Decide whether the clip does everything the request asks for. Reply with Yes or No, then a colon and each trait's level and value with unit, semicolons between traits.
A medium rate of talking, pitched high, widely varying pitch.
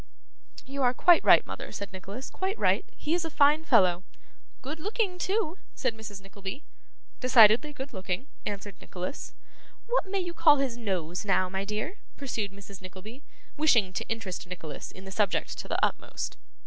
Yes: average, 170 wpm; high, 225 Hz; wide, 7.6 semitones